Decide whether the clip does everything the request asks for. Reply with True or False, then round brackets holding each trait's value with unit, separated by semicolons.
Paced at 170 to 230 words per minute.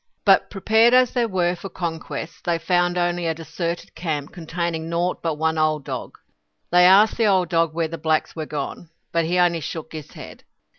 True (195 wpm)